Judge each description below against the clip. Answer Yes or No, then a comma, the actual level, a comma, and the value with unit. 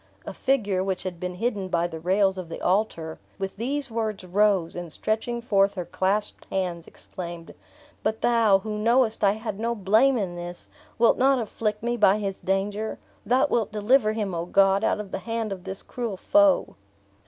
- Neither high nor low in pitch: No, high, 205 Hz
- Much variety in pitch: No, average, 3.3 semitones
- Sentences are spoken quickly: No, average, 190 wpm